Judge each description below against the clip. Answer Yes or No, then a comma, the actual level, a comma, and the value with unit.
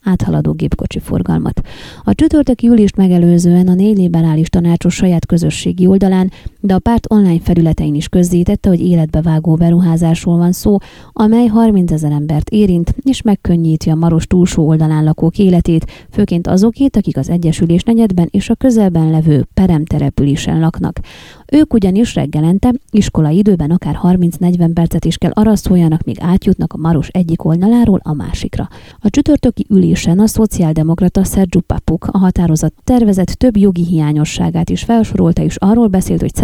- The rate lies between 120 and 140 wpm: No, average, 150 wpm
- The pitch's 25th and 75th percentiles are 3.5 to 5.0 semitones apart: Yes, average, 3.9 semitones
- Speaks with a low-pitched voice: No, medium, 175 Hz